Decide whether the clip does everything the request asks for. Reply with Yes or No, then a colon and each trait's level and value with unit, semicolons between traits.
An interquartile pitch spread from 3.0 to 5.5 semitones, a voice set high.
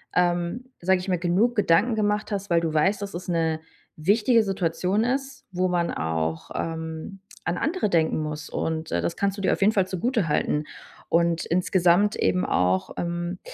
No: average, 3.8 semitones; medium, 180 Hz